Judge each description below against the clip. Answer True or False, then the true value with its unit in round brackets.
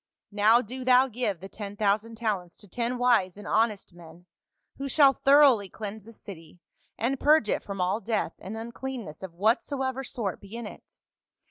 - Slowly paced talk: False (175 wpm)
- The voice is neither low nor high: False (220 Hz)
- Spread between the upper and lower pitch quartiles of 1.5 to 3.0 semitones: False (4.0 semitones)